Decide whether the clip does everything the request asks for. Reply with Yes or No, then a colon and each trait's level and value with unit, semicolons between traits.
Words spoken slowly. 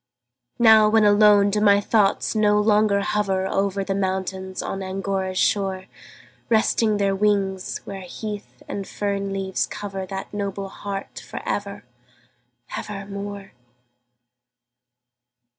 Yes: slow, 120 wpm